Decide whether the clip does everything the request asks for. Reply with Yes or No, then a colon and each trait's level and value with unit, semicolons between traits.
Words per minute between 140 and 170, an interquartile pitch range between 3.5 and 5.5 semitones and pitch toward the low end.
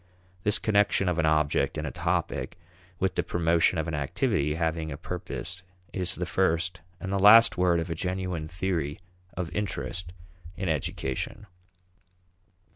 No: average, 150 wpm; average, 2.8 semitones; very low, 85 Hz